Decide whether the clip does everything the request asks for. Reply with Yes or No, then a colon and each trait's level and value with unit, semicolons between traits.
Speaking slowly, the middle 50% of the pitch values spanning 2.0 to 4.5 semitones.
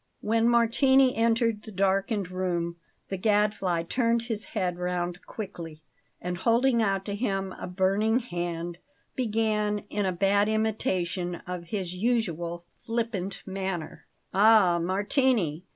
Yes: slow, 125 wpm; average, 4.0 semitones